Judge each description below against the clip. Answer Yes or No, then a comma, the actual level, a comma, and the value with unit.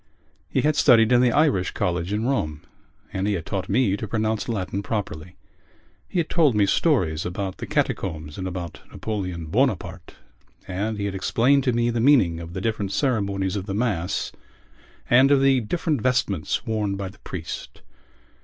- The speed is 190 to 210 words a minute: No, average, 175 wpm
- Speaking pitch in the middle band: No, low, 100 Hz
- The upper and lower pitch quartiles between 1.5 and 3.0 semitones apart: No, average, 4.7 semitones